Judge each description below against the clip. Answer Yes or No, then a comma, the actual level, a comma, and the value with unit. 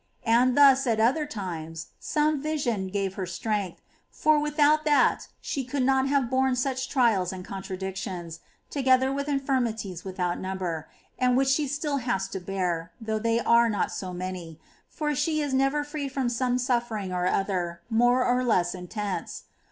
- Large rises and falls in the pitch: Yes, wide, 6.3 semitones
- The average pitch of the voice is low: No, high, 235 Hz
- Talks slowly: No, average, 170 wpm